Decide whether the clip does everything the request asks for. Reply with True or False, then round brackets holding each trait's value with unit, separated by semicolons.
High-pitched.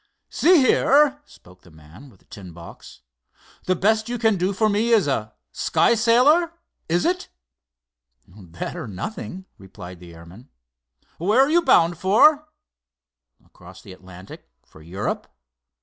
False (180 Hz)